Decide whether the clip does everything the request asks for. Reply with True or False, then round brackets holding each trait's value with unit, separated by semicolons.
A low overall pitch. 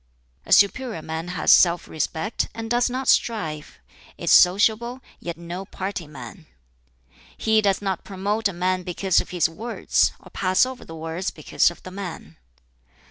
False (185 Hz)